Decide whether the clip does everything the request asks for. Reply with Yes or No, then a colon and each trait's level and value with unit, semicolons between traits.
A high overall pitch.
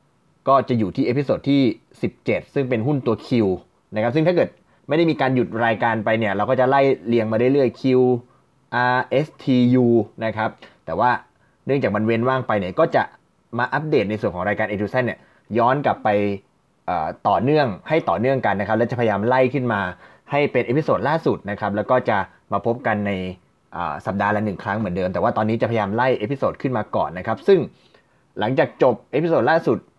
No: low, 115 Hz